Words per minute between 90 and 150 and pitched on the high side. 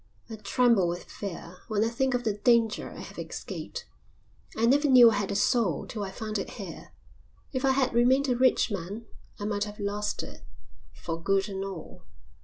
No: average, 200 wpm; high, 215 Hz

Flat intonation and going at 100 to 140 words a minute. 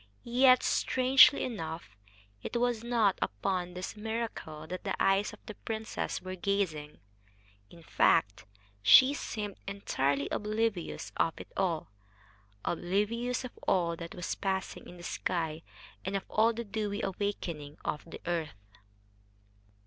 No: average, 4.8 semitones; slow, 135 wpm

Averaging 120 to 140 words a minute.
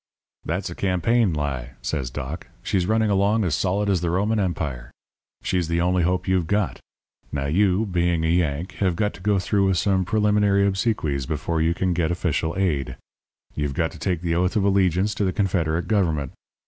No: average, 190 wpm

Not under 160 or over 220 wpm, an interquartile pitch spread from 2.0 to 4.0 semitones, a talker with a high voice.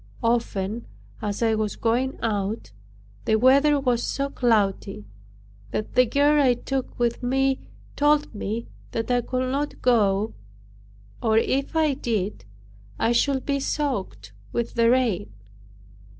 No: slow, 135 wpm; average, 3.7 semitones; high, 240 Hz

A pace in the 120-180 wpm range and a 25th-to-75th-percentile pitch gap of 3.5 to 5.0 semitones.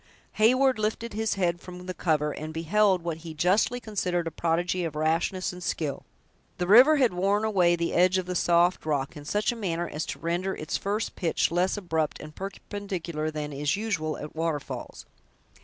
No: average, 190 wpm; average, 4.0 semitones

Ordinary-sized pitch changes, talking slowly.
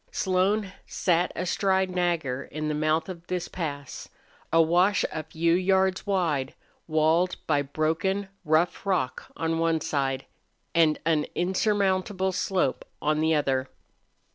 Yes: average, 3.2 semitones; slow, 130 wpm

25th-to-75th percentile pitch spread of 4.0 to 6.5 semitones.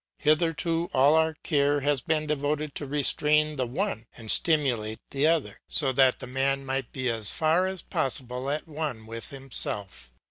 No: average, 3.2 semitones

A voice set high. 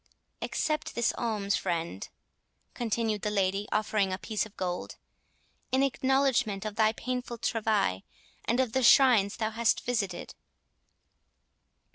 Yes: high, 220 Hz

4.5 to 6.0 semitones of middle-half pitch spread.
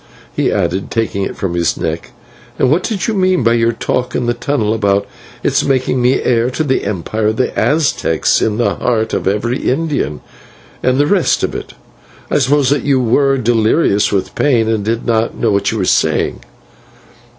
No: average, 4.1 semitones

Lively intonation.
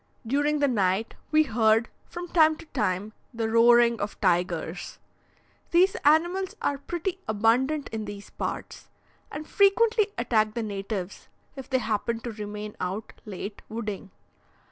Yes: wide, 6.3 semitones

